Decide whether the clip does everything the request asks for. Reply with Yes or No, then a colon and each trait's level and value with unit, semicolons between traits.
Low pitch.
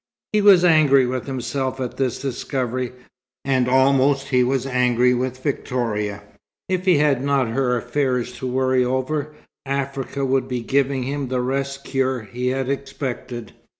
Yes: low, 130 Hz